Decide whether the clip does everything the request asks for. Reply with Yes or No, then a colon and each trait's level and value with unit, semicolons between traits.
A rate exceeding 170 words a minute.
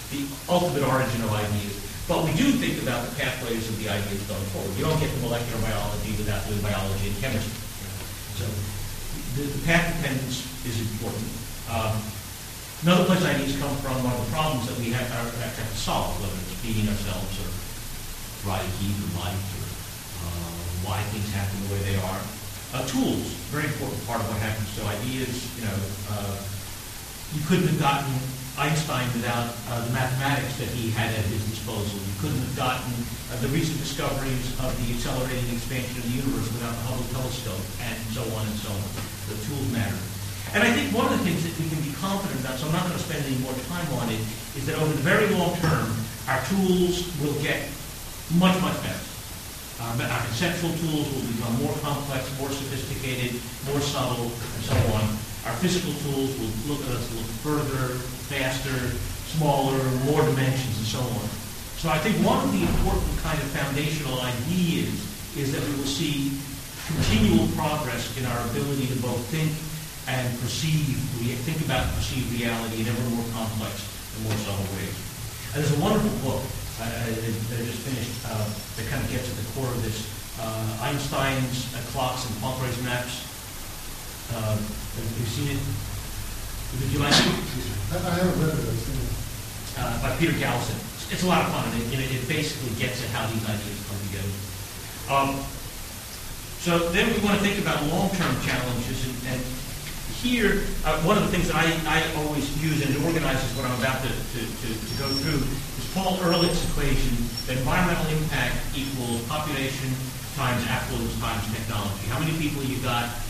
Yes: average, 180 wpm